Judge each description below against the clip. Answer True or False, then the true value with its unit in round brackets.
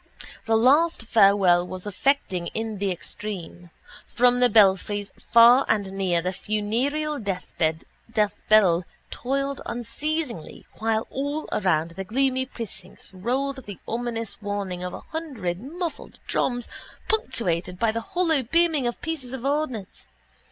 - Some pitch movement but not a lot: False (5.8 semitones)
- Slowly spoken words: True (125 wpm)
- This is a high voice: True (225 Hz)